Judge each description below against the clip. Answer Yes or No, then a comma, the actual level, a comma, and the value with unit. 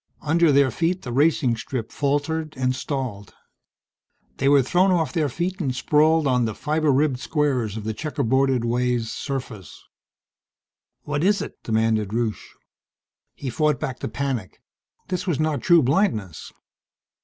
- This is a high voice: No, low, 135 Hz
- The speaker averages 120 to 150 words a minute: Yes, average, 145 wpm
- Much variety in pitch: No, average, 4.4 semitones